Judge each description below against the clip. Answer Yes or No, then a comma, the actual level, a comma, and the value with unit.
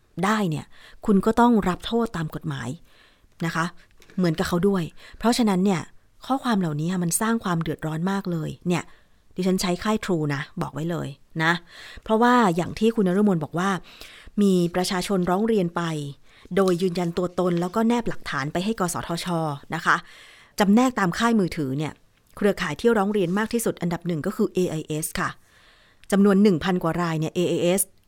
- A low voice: No, medium, 180 Hz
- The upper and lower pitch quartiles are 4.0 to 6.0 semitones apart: No, average, 3.4 semitones